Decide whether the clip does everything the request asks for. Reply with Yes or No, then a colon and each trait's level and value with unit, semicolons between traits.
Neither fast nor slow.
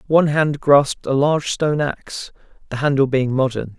Yes: average, 160 wpm